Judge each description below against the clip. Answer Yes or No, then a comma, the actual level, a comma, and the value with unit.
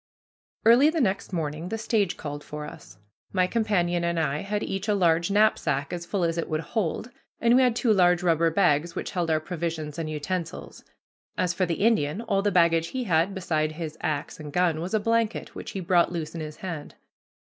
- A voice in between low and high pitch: Yes, medium, 175 Hz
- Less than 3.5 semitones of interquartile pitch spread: No, average, 4.0 semitones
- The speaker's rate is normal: No, fast, 210 wpm